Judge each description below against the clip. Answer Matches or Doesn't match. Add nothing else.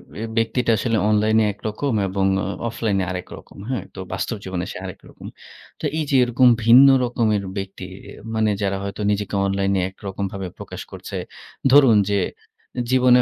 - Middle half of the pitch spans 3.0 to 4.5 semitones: Matches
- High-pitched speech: Doesn't match